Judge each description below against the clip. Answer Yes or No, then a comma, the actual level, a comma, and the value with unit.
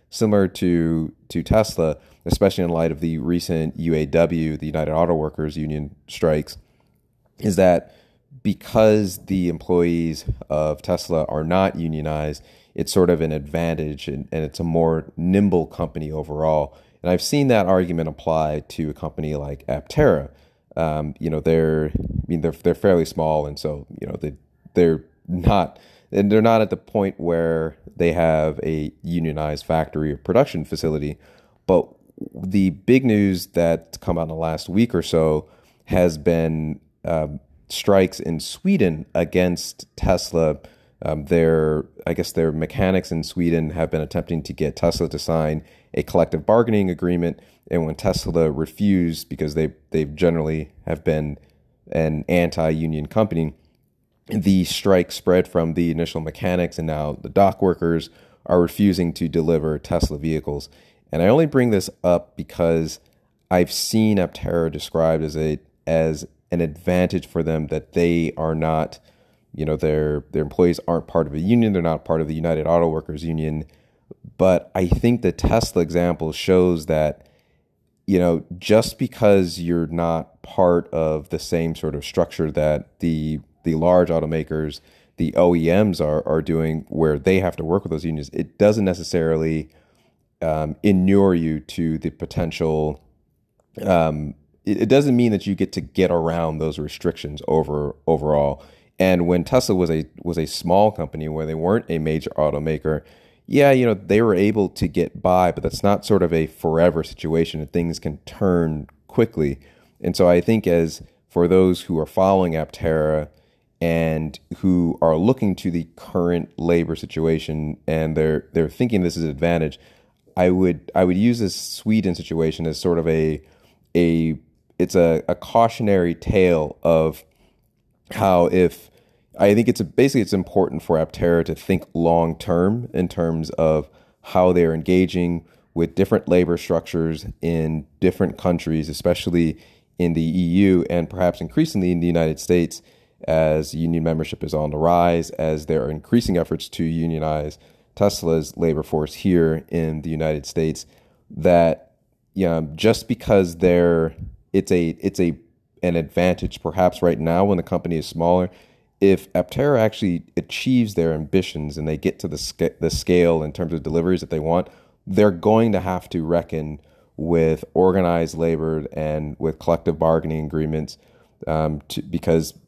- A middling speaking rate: Yes, average, 160 wpm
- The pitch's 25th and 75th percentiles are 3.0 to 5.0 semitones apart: No, narrow, 2.4 semitones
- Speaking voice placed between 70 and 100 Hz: Yes, very low, 80 Hz